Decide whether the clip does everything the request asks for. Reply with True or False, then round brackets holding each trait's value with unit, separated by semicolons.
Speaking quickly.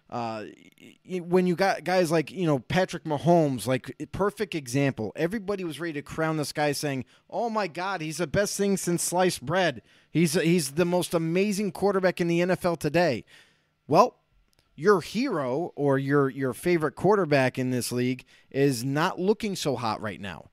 False (175 wpm)